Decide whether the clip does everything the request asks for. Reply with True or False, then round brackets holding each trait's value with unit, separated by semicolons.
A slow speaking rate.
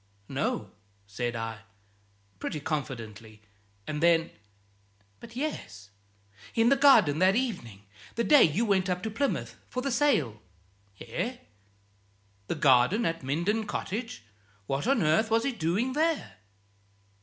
True (130 wpm)